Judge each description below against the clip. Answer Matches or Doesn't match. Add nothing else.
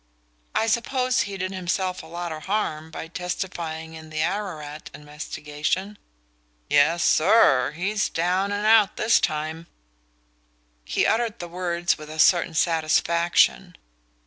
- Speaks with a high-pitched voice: Doesn't match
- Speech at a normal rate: Doesn't match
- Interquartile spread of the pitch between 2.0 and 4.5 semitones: Matches